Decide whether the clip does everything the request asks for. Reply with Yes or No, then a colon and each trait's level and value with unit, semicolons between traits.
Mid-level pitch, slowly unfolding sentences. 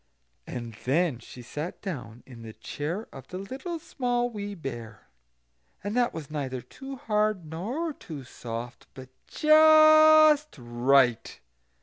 Yes: medium, 170 Hz; slow, 130 wpm